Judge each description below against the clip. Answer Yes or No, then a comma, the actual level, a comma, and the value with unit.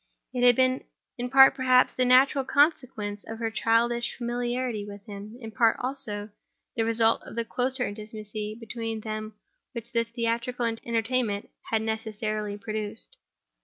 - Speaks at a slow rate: No, average, 145 wpm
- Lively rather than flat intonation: No, narrow, 2.4 semitones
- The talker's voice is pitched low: No, high, 230 Hz